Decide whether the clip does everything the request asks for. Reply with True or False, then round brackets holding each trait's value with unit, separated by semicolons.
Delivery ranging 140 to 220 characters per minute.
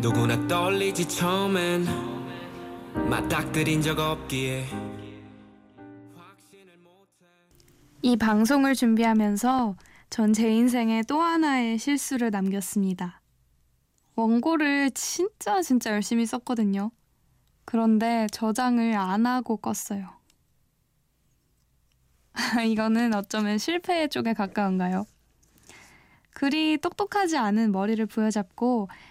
True (190 characters per minute)